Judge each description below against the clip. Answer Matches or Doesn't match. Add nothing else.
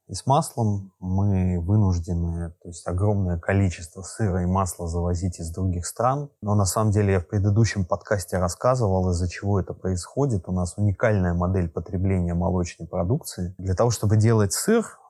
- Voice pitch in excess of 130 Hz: Doesn't match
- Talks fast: Matches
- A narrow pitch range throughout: Doesn't match